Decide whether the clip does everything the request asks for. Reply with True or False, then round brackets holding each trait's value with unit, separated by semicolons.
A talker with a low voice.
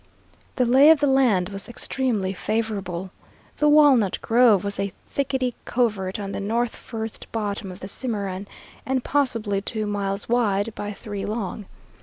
False (215 Hz)